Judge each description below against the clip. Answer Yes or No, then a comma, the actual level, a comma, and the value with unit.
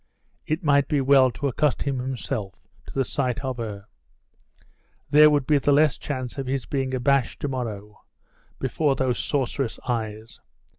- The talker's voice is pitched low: Yes, low, 130 Hz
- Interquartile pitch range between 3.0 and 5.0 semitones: No, narrow, 2.6 semitones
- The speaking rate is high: No, average, 155 wpm